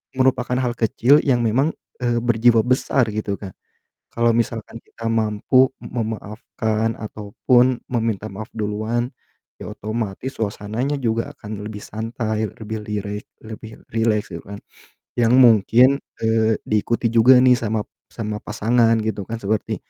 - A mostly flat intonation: Yes, narrow, 2.1 semitones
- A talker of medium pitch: No, low, 115 Hz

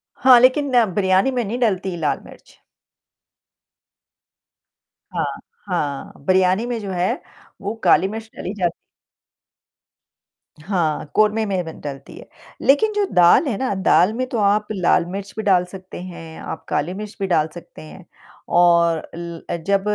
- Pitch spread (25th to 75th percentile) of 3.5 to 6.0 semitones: Yes, average, 3.8 semitones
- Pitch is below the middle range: No, high, 190 Hz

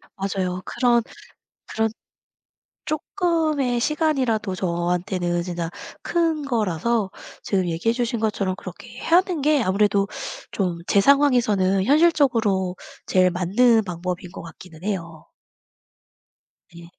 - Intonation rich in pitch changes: Yes, wide, 6.1 semitones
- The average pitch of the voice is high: Yes, high, 205 Hz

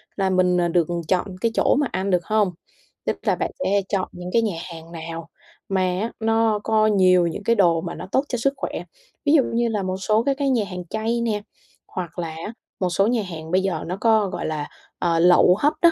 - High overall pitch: Yes, high, 195 Hz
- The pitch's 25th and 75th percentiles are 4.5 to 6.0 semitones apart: No, average, 4.1 semitones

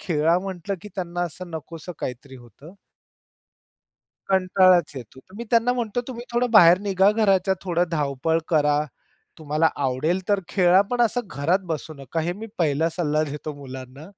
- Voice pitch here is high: No, medium, 170 Hz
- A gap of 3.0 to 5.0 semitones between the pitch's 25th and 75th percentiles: Yes, average, 4.5 semitones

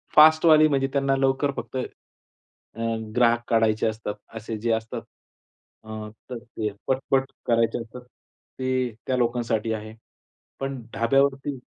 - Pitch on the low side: Yes, low, 125 Hz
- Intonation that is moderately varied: Yes, average, 3.2 semitones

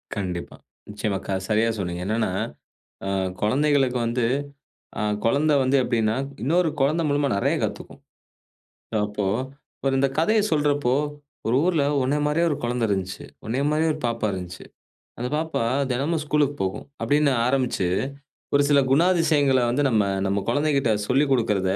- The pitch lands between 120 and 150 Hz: Yes, low, 135 Hz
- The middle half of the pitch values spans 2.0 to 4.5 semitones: No, average, 5.1 semitones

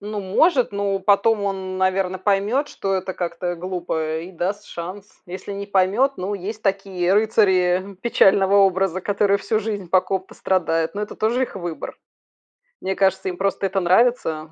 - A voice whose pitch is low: No, high, 195 Hz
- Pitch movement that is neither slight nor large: No, narrow, 1.9 semitones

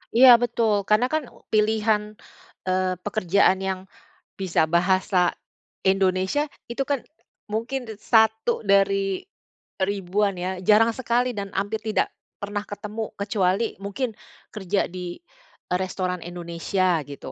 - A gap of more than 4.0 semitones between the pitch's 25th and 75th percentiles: No, average, 3.0 semitones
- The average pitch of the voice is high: Yes, high, 200 Hz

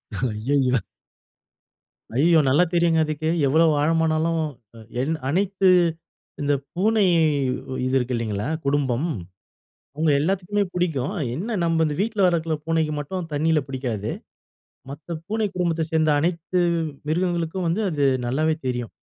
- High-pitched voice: No, medium, 160 Hz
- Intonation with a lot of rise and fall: No, average, 3.8 semitones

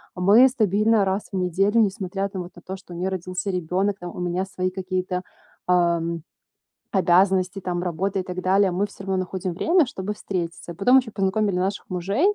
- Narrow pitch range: Yes, narrow, 1.8 semitones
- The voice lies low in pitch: No, high, 190 Hz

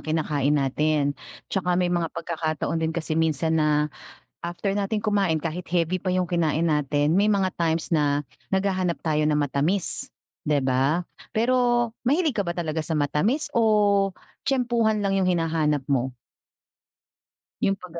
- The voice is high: No, medium, 170 Hz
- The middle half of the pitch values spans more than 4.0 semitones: Yes, average, 4.4 semitones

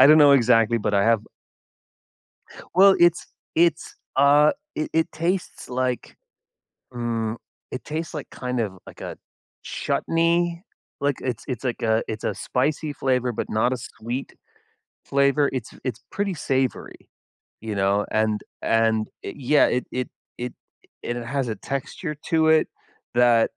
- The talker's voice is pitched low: Yes, low, 130 Hz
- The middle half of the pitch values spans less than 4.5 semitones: No, average, 4.8 semitones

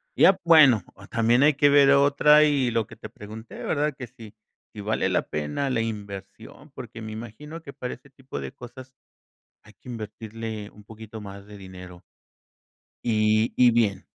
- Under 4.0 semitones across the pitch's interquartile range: No, average, 4.5 semitones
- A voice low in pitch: Yes, low, 115 Hz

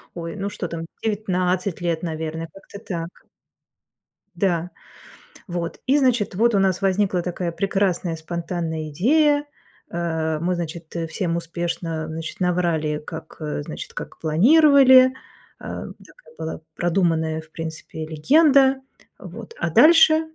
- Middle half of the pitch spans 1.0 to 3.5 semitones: No, average, 4.1 semitones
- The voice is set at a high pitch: No, medium, 175 Hz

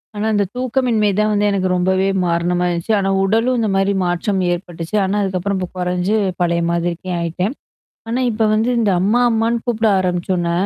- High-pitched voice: Yes, high, 195 Hz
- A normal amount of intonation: Yes, average, 3.6 semitones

